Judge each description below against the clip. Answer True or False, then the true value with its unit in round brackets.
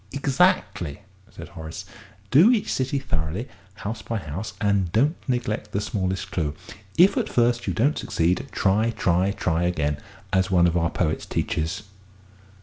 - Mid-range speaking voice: False (100 Hz)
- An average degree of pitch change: False (6.1 semitones)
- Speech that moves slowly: False (160 wpm)